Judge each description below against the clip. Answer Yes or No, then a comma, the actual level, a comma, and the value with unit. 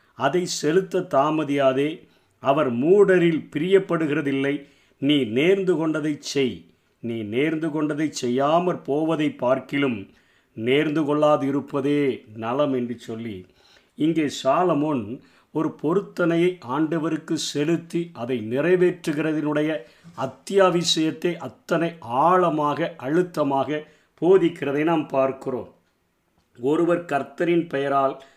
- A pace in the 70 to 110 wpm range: Yes, average, 80 wpm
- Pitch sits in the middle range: Yes, medium, 150 Hz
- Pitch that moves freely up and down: No, average, 3.7 semitones